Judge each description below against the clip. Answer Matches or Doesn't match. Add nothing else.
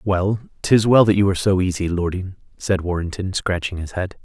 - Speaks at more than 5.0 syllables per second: Matches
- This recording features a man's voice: Matches